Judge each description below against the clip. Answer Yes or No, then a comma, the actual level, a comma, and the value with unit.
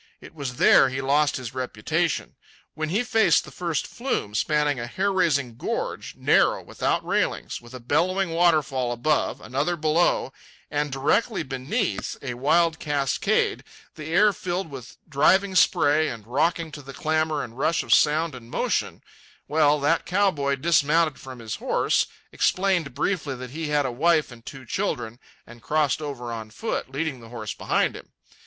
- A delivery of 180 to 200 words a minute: No, average, 165 wpm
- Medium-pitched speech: Yes, medium, 150 Hz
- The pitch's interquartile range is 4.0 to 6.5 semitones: Yes, average, 4.4 semitones